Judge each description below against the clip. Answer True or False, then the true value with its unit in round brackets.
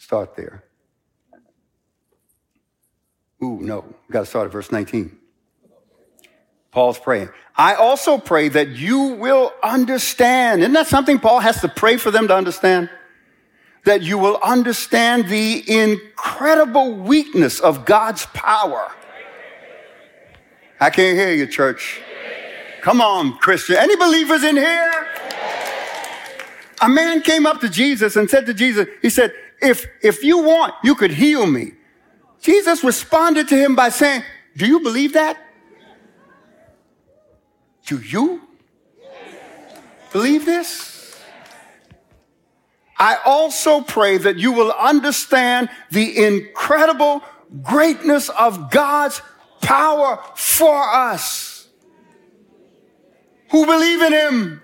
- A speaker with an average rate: False (115 wpm)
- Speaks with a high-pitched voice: True (275 Hz)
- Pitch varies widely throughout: True (5.9 semitones)